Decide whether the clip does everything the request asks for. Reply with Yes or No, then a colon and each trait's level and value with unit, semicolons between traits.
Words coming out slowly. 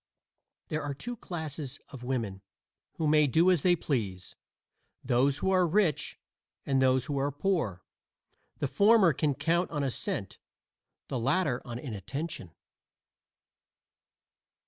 Yes: slow, 125 wpm